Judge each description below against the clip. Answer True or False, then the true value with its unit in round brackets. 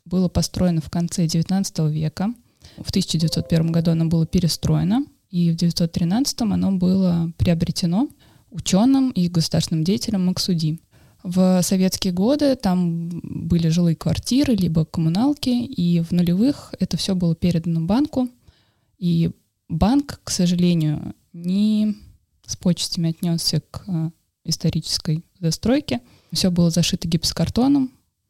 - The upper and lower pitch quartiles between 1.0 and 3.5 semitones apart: True (2.9 semitones)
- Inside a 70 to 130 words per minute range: True (115 wpm)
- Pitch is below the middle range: False (175 Hz)